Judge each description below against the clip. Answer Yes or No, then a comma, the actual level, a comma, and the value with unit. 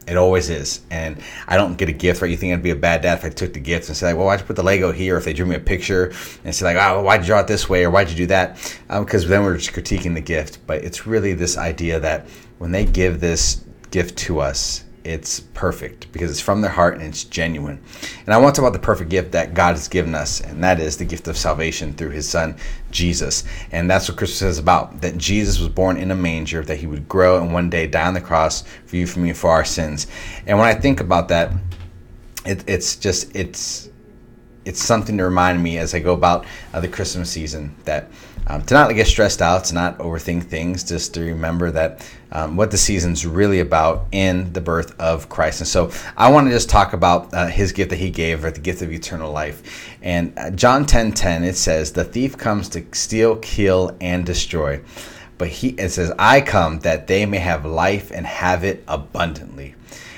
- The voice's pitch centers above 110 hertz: No, very low, 90 Hz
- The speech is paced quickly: Yes, fast, 240 wpm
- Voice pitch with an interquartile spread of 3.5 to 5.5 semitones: No, narrow, 2.5 semitones